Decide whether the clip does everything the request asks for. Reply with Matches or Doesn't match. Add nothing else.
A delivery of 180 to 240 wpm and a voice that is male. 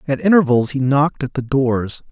Matches